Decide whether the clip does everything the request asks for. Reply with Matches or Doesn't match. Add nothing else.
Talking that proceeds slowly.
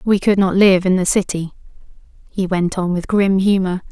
Doesn't match